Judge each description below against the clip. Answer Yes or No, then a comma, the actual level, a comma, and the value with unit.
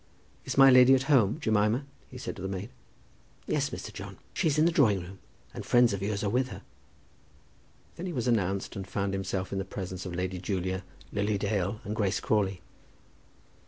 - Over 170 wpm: Yes, average, 200 wpm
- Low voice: Yes, low, 100 Hz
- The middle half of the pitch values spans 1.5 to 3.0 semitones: No, average, 4.4 semitones